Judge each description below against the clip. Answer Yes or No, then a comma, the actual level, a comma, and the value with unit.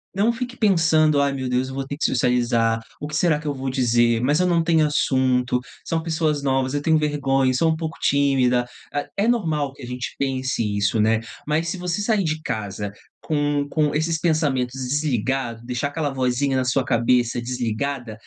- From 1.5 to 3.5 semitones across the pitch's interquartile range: No, average, 3.9 semitones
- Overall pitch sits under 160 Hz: Yes, medium, 140 Hz